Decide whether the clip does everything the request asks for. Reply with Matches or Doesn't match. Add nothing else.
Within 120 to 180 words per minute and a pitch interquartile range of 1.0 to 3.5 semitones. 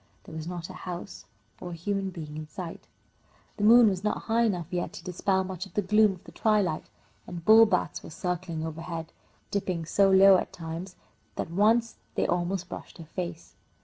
Doesn't match